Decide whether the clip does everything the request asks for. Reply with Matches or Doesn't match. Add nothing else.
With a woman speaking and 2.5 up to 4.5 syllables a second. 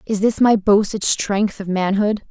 Matches